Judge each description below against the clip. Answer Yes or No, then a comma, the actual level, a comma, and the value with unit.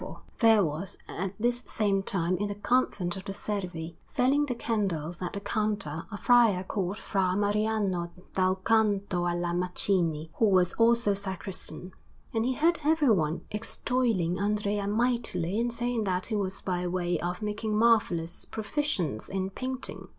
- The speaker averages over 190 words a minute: No, average, 160 wpm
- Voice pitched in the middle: No, high, 200 Hz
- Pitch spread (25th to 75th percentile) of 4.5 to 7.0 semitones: No, average, 3.8 semitones